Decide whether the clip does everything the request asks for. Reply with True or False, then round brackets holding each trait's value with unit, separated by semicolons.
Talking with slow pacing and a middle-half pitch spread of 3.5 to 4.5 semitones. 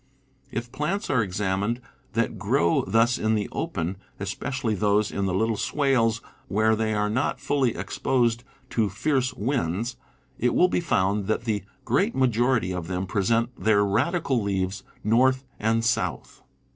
False (150 wpm; 3.8 semitones)